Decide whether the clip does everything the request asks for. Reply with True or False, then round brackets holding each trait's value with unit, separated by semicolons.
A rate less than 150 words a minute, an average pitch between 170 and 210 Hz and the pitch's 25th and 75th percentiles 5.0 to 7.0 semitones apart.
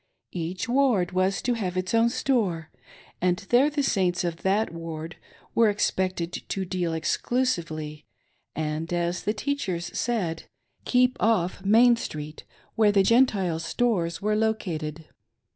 True (140 wpm; 185 Hz; 5.3 semitones)